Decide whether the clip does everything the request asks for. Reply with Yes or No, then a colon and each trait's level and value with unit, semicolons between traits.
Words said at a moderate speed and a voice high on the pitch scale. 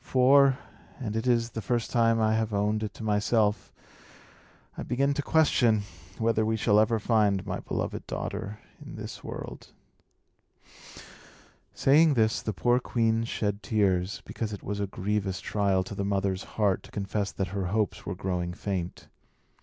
No: average, 160 wpm; low, 105 Hz